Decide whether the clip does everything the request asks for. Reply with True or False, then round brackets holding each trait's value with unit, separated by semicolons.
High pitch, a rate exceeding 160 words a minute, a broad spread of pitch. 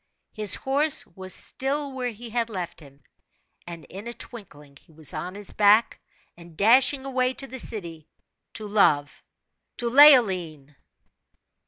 False (210 Hz; 145 wpm; 7.0 semitones)